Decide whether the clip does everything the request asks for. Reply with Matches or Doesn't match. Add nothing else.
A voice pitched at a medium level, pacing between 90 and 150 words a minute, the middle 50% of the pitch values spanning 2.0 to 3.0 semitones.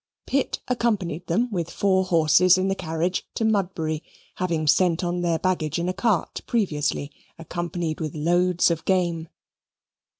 Matches